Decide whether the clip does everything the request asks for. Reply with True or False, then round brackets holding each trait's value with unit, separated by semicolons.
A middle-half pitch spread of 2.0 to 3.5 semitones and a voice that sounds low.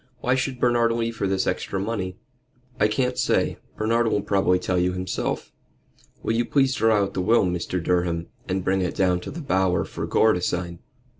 False (4.2 semitones; 95 Hz)